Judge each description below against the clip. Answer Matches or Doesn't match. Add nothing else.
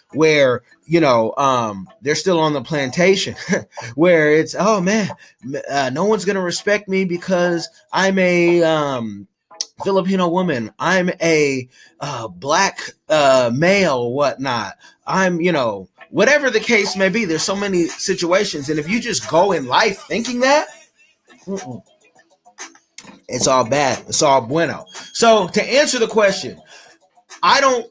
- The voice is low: Doesn't match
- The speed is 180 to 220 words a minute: Doesn't match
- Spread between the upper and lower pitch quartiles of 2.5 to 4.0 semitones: Doesn't match